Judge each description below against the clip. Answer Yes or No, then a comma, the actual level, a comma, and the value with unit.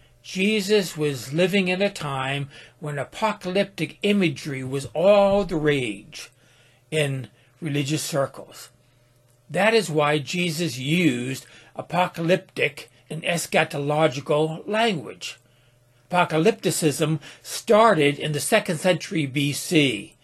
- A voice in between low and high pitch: Yes, medium, 155 Hz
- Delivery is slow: Yes, slow, 95 wpm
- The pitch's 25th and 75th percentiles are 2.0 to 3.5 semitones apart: No, average, 5.1 semitones